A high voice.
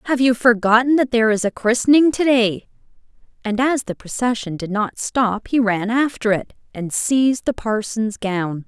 Yes: high, 230 Hz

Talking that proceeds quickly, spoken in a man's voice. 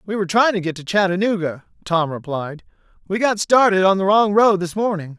Yes: fast, 210 wpm; male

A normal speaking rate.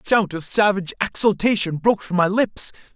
Yes: average, 185 wpm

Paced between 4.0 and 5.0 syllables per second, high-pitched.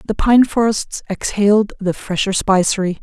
Yes: 4.8 syllables/s; high, 200 Hz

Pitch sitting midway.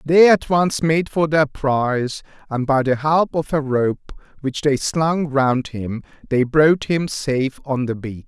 Yes: medium, 145 Hz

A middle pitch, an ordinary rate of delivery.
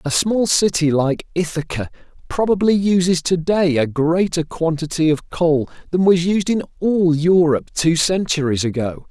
Yes: medium, 165 Hz; average, 150 wpm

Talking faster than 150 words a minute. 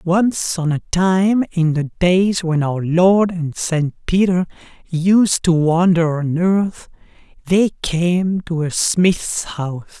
No: average, 145 wpm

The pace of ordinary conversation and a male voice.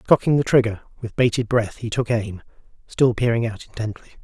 Yes: average, 185 wpm; male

